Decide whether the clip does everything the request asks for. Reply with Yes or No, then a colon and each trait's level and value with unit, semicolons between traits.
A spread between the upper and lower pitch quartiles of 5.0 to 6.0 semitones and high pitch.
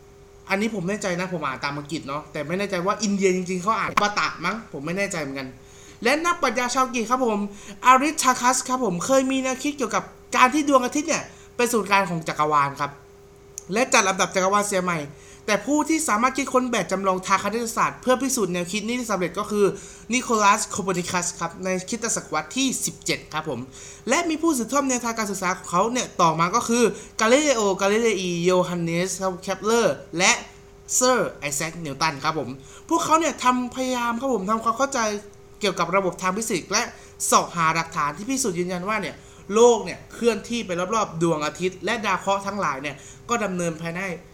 Yes: wide, 5.4 semitones; high, 200 Hz